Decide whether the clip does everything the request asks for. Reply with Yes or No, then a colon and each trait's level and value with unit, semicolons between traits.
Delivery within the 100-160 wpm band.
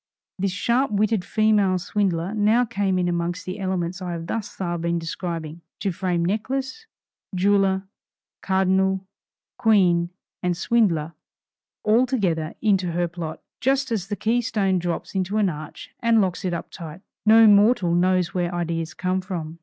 Yes: average, 155 wpm